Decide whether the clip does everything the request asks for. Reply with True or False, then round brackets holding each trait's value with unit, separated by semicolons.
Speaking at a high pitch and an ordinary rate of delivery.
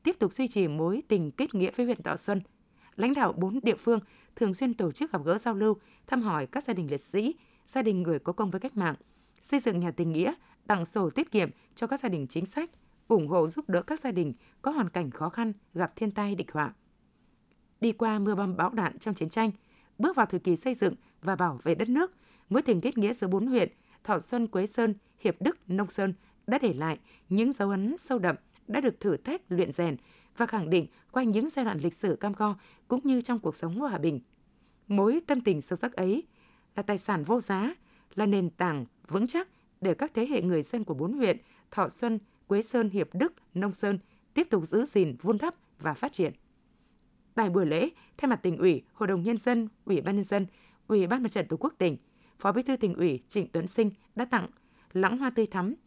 True (210 Hz; 235 wpm)